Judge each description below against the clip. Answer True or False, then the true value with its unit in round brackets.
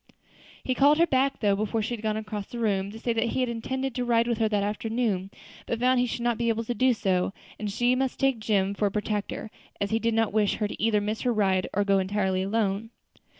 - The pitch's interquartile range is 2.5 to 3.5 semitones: True (2.8 semitones)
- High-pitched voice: True (220 Hz)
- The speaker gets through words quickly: True (260 wpm)